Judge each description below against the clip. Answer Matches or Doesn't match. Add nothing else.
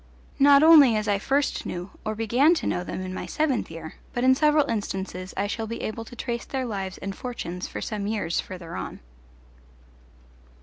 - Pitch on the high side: Matches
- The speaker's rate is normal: Matches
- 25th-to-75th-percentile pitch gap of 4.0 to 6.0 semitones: Matches